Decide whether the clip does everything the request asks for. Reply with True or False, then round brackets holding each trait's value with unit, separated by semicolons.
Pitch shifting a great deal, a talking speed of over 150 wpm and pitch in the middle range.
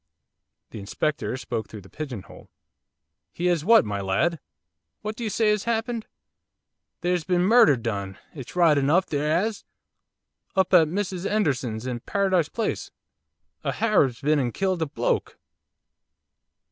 False (7.5 semitones; 145 wpm; 165 Hz)